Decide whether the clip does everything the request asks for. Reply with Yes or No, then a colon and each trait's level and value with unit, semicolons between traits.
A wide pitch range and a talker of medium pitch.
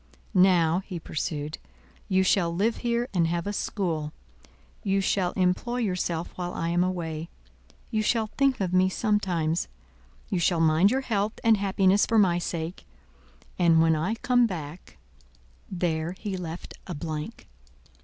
No: average, 3.5 semitones; medium, 180 Hz